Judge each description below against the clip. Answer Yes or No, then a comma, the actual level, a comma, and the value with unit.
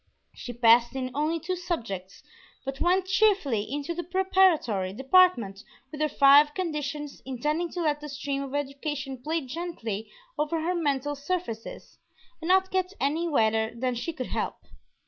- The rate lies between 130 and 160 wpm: Yes, average, 155 wpm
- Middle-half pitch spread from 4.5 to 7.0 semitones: Yes, average, 5.1 semitones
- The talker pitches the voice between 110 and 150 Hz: No, very high, 290 Hz